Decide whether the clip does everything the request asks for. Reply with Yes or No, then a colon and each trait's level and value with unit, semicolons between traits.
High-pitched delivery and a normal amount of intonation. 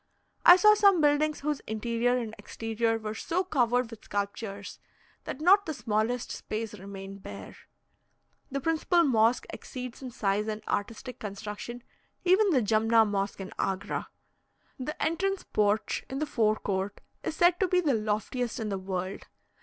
No: high, 230 Hz; wide, 6.2 semitones